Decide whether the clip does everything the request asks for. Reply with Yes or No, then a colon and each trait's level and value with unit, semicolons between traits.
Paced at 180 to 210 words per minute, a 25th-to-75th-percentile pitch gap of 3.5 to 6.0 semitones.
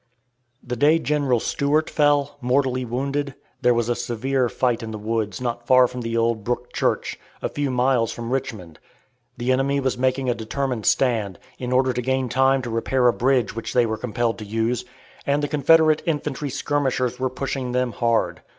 No: average, 185 wpm; narrow, 2.5 semitones